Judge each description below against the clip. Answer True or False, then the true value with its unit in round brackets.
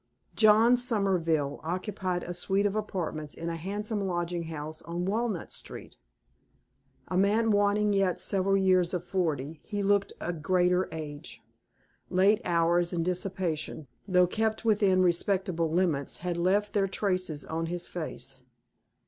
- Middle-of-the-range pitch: True (180 Hz)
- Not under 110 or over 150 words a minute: True (140 wpm)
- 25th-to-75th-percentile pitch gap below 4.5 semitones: True (3.1 semitones)